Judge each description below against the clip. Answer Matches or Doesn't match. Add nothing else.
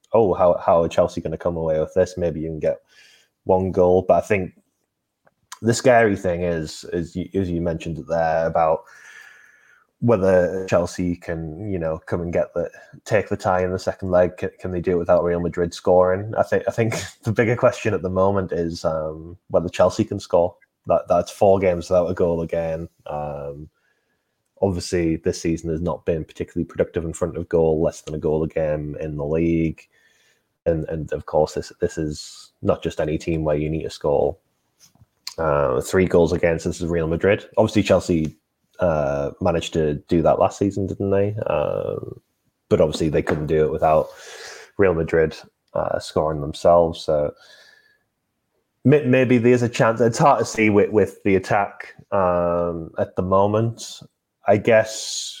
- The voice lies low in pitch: Matches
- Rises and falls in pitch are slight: Doesn't match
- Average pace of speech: Matches